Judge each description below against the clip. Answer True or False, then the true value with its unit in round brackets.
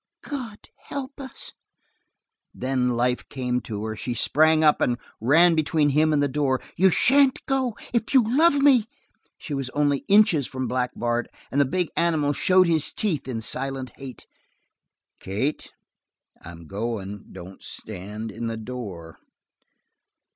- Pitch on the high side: False (140 Hz)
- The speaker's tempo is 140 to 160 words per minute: True (145 wpm)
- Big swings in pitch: True (6.8 semitones)